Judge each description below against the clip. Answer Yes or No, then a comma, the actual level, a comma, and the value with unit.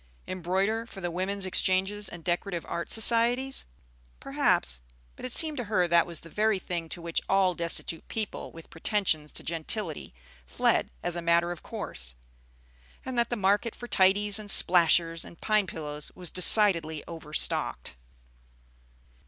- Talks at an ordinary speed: Yes, average, 155 wpm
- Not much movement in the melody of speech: No, average, 3.8 semitones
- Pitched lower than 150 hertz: No, medium, 185 Hz